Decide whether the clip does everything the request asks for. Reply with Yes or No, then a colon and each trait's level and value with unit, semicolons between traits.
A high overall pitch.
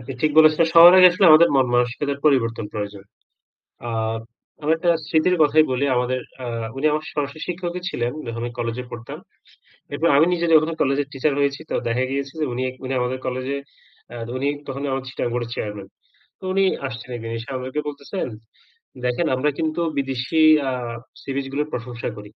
No: low, 135 Hz